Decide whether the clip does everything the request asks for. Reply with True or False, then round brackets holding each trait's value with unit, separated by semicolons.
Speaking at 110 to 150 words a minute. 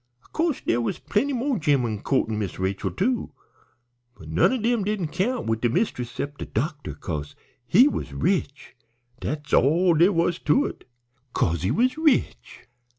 False (170 wpm)